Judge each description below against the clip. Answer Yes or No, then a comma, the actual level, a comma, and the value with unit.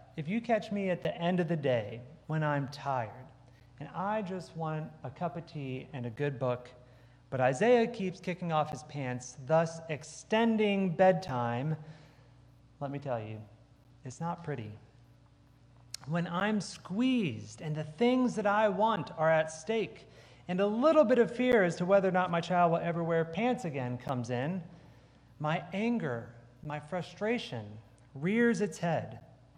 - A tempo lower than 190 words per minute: Yes, average, 165 wpm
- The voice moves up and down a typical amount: No, wide, 6.8 semitones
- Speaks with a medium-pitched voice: Yes, medium, 155 Hz